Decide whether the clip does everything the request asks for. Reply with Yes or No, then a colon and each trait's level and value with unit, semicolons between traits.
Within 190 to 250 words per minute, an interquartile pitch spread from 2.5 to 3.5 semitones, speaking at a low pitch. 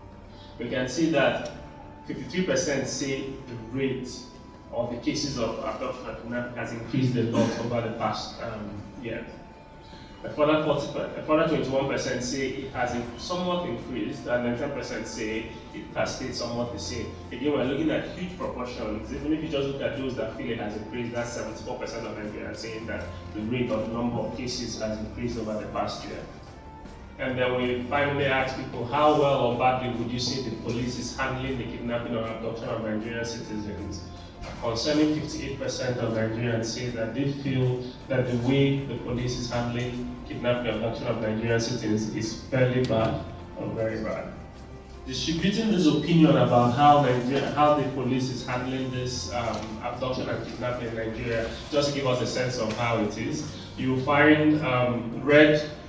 No: average, 175 wpm; average, 2.9 semitones; low, 120 Hz